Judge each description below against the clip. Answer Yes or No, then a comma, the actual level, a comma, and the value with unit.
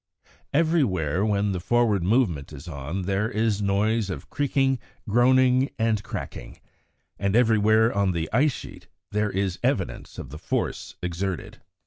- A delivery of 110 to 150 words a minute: Yes, average, 140 wpm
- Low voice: Yes, low, 105 Hz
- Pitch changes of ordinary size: Yes, average, 4.4 semitones